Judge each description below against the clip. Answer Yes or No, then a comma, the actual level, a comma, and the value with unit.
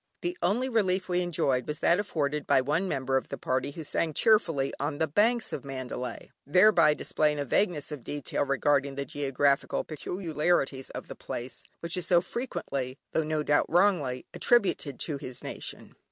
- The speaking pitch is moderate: Yes, medium, 150 Hz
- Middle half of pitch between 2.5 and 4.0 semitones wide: No, average, 4.5 semitones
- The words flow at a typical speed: Yes, average, 175 wpm